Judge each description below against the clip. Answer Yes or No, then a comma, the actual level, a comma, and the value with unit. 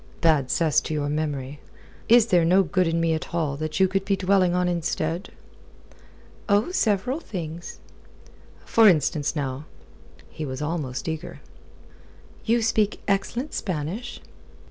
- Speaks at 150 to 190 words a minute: No, average, 140 wpm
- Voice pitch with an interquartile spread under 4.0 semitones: No, average, 4.3 semitones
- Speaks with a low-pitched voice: No, medium, 170 Hz